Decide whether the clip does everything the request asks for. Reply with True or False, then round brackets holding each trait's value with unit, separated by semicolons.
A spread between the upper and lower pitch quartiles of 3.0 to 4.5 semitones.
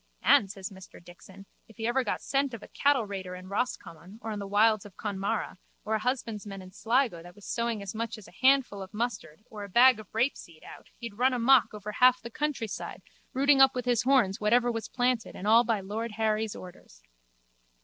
True (3.6 semitones)